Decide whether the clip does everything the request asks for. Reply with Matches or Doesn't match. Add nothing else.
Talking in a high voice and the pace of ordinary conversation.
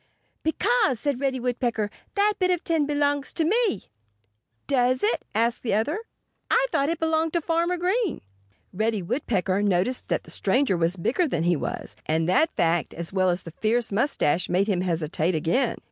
Matches